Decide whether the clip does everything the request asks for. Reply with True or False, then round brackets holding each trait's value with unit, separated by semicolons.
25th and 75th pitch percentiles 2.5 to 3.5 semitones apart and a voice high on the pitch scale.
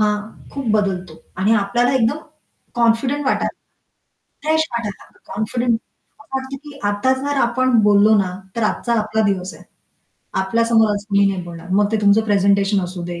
True (3.2 semitones; 215 Hz)